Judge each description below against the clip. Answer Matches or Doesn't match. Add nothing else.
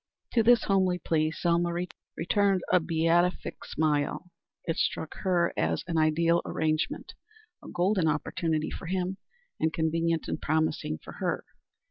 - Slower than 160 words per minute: Matches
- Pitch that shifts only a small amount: Matches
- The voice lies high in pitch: Doesn't match